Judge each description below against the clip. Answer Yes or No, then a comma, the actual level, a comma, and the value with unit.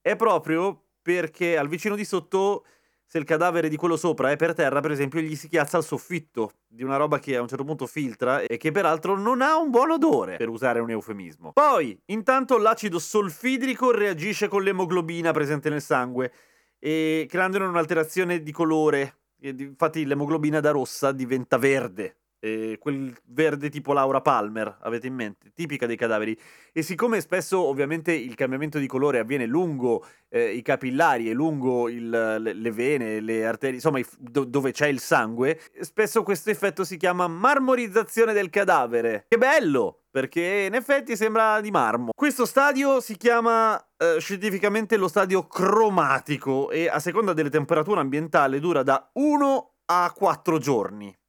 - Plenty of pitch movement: Yes, wide, 6.9 semitones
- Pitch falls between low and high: Yes, medium, 160 Hz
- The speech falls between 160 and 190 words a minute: Yes, average, 165 wpm